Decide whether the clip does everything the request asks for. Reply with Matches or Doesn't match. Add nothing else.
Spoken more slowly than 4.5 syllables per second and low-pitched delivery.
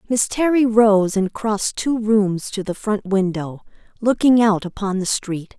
Doesn't match